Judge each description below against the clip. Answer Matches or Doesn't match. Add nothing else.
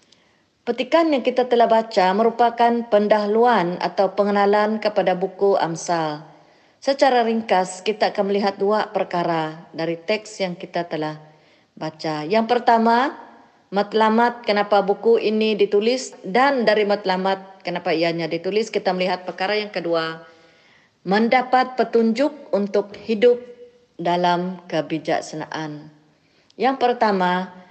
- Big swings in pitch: Doesn't match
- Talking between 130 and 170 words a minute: Doesn't match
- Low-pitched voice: Doesn't match